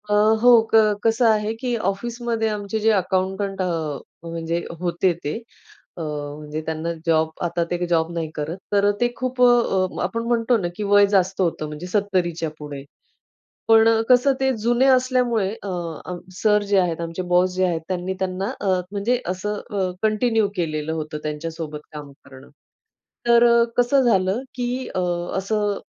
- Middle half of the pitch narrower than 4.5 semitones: No, average, 4.9 semitones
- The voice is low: No, high, 190 Hz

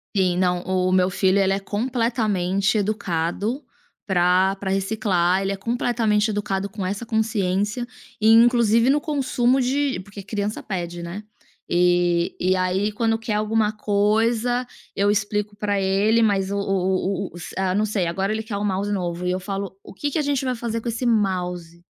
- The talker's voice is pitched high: Yes, high, 205 Hz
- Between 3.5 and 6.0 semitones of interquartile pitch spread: No, average, 3.1 semitones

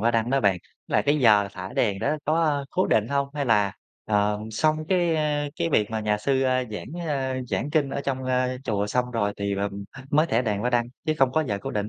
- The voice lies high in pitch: No, low, 125 Hz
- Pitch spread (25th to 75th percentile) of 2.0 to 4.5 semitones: No, wide, 5.5 semitones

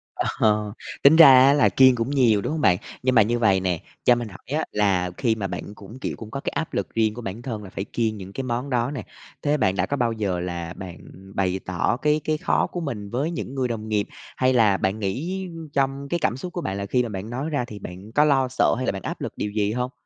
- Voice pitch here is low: Yes, low, 115 Hz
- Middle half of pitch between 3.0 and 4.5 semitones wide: No, average, 5.1 semitones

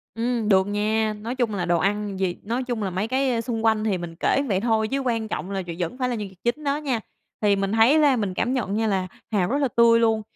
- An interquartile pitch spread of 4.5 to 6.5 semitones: No, average, 3.6 semitones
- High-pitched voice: Yes, high, 220 Hz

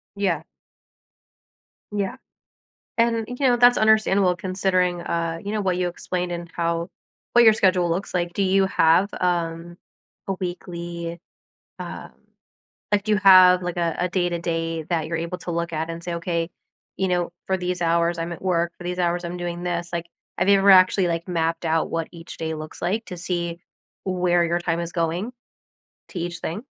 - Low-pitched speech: No, medium, 175 Hz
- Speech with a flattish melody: Yes, narrow, 1.7 semitones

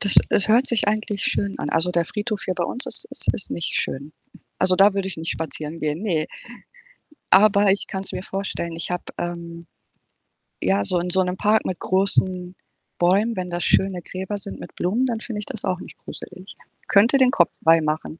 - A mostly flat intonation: No, average, 3.2 semitones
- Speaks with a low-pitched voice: No, medium, 185 Hz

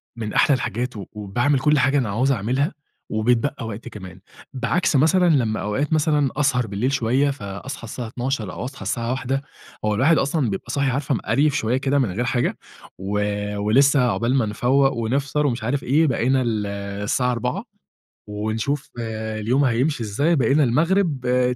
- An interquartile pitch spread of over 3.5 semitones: Yes, average, 3.9 semitones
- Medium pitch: No, low, 125 Hz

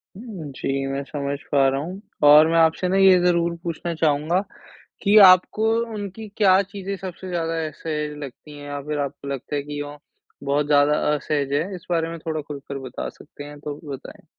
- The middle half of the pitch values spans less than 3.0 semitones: No, average, 3.7 semitones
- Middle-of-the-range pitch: Yes, medium, 155 Hz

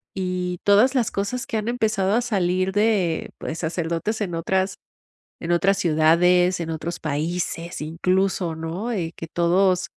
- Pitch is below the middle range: No, medium, 180 Hz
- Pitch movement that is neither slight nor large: Yes, average, 3.0 semitones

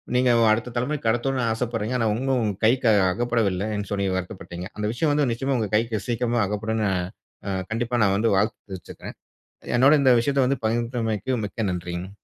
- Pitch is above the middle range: No, low, 115 Hz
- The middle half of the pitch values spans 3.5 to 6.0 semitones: No, average, 3.0 semitones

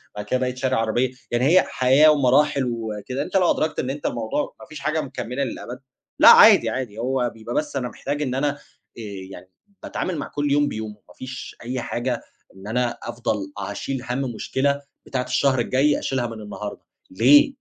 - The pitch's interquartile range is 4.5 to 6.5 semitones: No, average, 3.3 semitones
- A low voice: Yes, low, 130 Hz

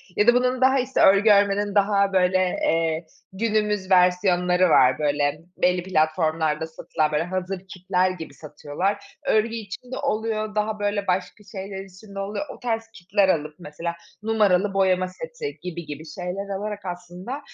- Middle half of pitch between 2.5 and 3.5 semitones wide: Yes, average, 3.0 semitones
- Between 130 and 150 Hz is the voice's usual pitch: No, high, 190 Hz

